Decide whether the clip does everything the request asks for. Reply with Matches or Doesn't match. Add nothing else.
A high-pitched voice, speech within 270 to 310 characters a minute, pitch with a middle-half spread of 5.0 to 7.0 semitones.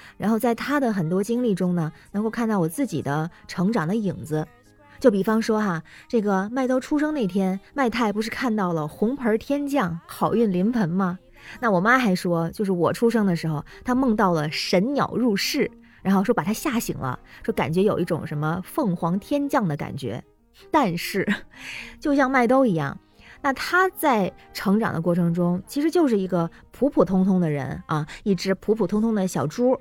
Matches